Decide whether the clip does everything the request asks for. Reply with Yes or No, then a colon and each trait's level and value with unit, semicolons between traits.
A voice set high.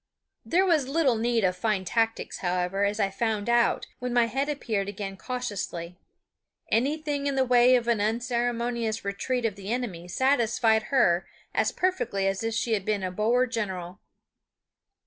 Yes: high, 225 Hz